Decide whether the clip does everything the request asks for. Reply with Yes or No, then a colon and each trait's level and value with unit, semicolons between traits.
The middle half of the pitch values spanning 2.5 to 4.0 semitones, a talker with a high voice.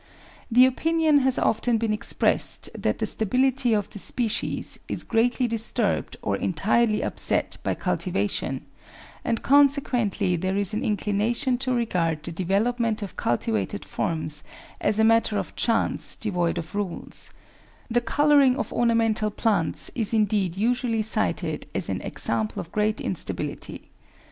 Yes: average, 3.4 semitones; high, 220 Hz